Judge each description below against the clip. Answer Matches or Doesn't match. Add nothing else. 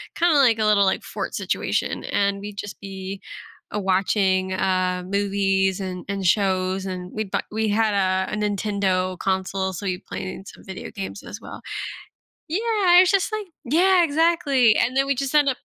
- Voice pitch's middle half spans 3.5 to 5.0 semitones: Doesn't match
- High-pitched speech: Matches